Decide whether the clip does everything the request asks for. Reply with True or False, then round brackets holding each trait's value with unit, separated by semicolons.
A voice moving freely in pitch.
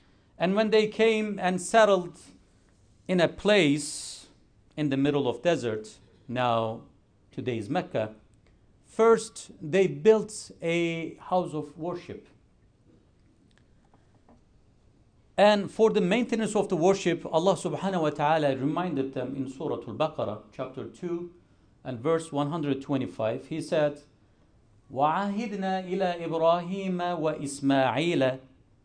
True (6.2 semitones)